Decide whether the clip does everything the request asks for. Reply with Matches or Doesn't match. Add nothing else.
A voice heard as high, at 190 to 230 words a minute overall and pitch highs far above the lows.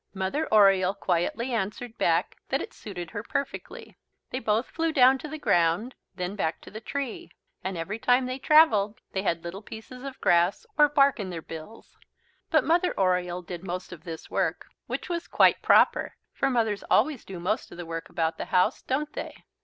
Matches